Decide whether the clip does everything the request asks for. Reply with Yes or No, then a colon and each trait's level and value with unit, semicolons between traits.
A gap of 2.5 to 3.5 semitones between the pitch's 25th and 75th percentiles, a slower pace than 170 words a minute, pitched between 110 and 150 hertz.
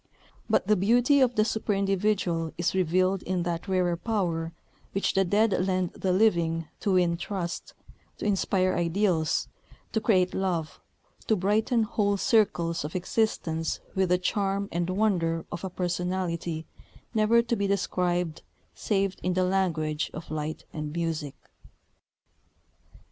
No: average, 3.1 semitones; average, 140 wpm; medium, 185 Hz